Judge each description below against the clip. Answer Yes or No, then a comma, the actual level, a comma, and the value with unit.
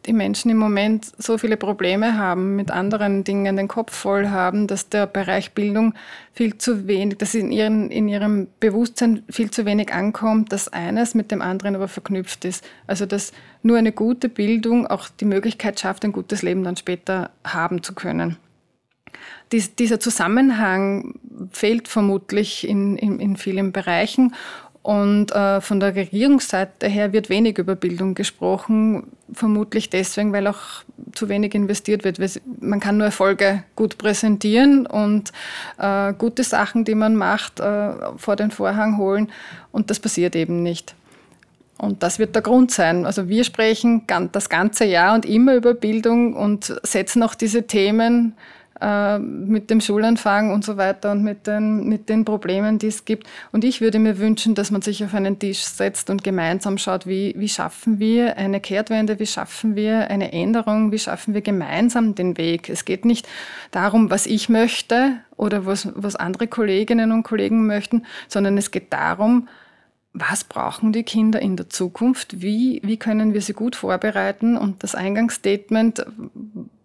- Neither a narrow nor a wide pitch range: No, narrow, 2.2 semitones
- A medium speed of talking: Yes, average, 170 wpm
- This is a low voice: No, high, 210 Hz